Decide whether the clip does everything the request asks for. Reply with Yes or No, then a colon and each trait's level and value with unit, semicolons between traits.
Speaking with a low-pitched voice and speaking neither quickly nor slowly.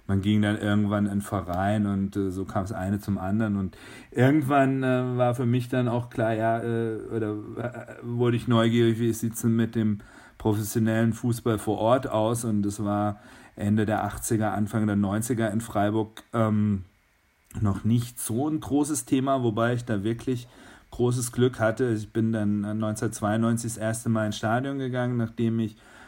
Yes: low, 110 Hz; average, 175 wpm